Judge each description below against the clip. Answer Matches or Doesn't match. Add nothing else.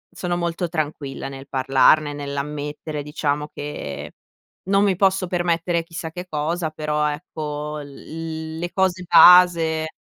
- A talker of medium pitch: Matches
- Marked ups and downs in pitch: Doesn't match